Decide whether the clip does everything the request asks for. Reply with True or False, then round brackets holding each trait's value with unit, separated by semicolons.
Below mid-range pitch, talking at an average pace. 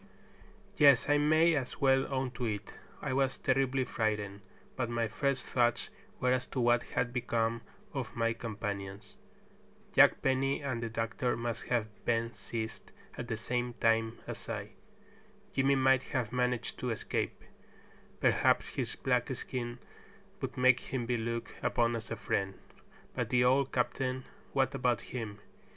True (120 Hz; 155 wpm)